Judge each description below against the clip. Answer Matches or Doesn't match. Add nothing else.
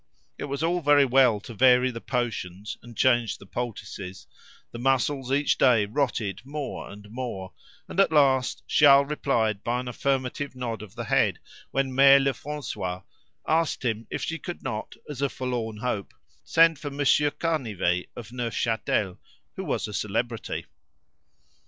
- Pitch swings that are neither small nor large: Matches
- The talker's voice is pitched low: Matches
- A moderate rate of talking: Matches